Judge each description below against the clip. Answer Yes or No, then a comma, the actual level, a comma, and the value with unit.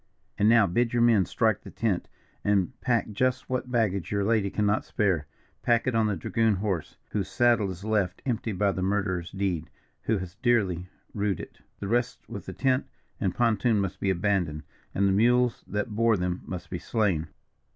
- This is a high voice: No, low, 105 Hz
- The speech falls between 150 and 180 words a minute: No, average, 190 wpm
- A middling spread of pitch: Yes, average, 3.6 semitones